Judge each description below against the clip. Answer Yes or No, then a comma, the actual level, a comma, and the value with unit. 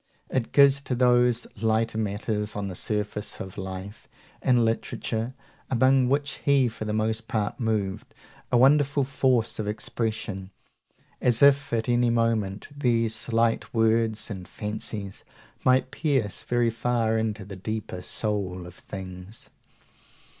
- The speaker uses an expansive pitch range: No, average, 2.8 semitones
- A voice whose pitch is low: Yes, low, 115 Hz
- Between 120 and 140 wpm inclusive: Yes, slow, 135 wpm